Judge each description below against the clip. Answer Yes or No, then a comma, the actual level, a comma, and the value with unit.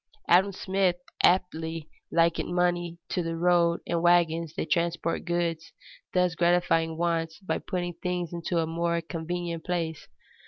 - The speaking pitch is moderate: Yes, medium, 170 Hz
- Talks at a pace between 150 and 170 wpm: No, average, 140 wpm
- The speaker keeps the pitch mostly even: Yes, narrow, 1.2 semitones